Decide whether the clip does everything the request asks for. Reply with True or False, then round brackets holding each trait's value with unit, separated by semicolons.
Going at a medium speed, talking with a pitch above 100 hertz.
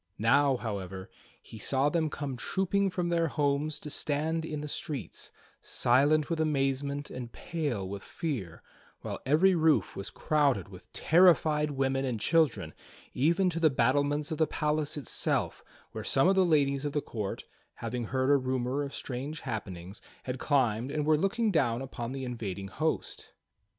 True (160 wpm; 140 Hz)